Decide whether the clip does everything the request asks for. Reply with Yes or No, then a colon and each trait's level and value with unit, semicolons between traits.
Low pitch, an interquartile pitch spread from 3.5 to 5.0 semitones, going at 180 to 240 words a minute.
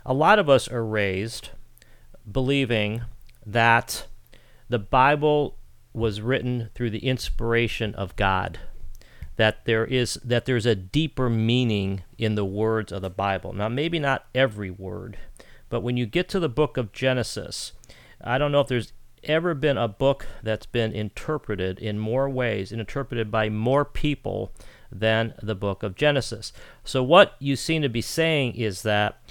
No: low, 115 Hz; average, 3.8 semitones; average, 160 wpm